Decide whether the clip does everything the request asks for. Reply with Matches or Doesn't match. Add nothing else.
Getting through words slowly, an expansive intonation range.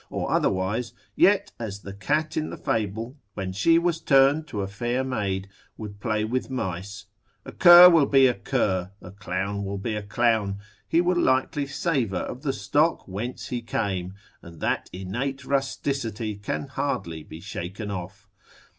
Doesn't match